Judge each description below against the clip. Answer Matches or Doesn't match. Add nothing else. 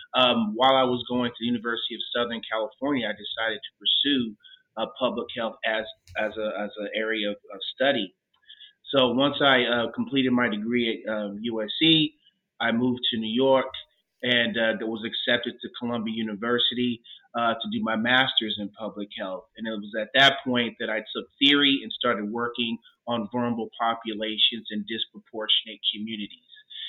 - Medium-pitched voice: Doesn't match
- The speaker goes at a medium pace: Matches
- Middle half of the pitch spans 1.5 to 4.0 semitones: Matches